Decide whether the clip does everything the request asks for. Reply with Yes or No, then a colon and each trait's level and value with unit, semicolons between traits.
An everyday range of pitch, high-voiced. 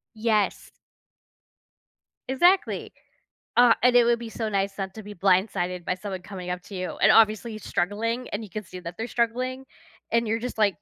Yes: average, 3.7 semitones; high, 215 Hz